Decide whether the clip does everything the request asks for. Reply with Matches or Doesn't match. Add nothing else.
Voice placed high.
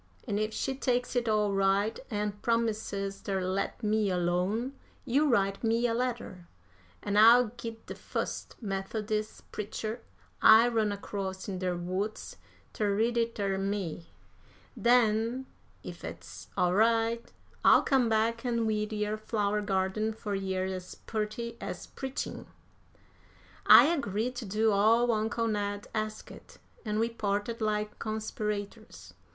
Matches